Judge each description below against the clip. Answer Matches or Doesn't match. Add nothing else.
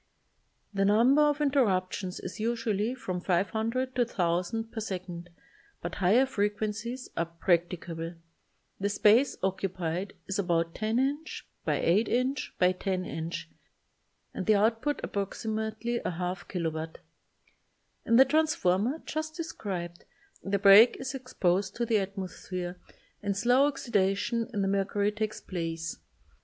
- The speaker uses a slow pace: Matches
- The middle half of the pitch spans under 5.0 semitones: Matches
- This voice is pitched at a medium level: Doesn't match